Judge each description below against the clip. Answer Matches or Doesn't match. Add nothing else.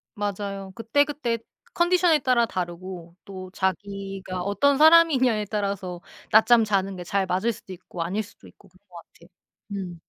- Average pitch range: Matches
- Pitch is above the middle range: Matches